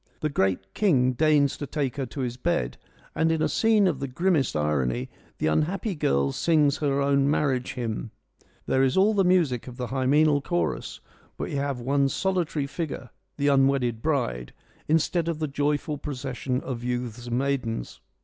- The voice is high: No, medium, 140 Hz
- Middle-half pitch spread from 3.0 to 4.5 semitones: Yes, average, 3.7 semitones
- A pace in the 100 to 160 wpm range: No, average, 180 wpm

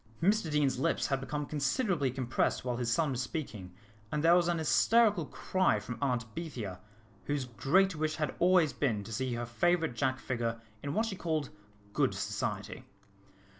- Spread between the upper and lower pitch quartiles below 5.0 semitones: No, average, 5.3 semitones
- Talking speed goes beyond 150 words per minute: Yes, average, 170 wpm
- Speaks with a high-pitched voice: No, medium, 145 Hz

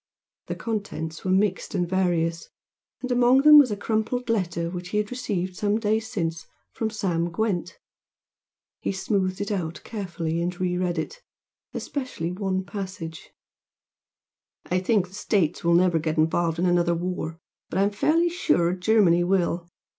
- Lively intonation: No, average, 3.7 semitones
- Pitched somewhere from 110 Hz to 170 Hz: No, medium, 185 Hz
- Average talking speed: Yes, average, 160 wpm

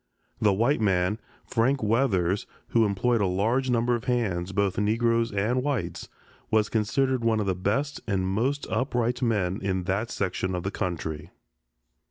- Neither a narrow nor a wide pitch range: Yes, average, 4.1 semitones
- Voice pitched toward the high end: No, low, 110 Hz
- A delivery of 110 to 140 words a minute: No, average, 160 wpm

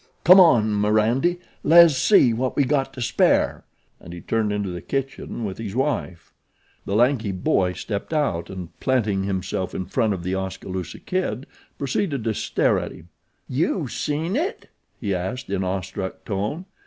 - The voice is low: Yes, low, 110 Hz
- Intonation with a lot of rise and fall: Yes, wide, 6.3 semitones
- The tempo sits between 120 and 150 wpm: No, average, 165 wpm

